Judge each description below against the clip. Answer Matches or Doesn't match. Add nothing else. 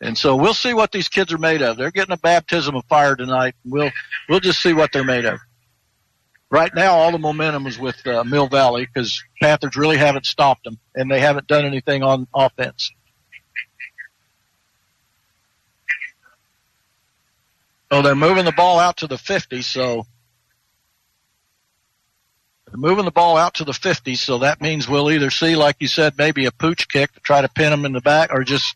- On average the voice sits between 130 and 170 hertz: Matches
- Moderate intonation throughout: Matches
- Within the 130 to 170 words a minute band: Doesn't match